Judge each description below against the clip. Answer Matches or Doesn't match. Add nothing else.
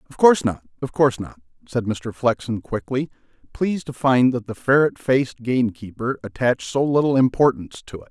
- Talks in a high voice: Doesn't match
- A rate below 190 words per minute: Matches